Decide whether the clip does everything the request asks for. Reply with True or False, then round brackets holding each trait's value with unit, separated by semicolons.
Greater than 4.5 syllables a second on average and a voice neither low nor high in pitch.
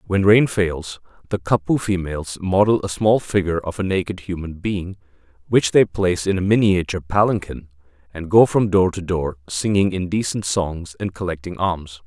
False (5.2 syllables/s; 90 Hz)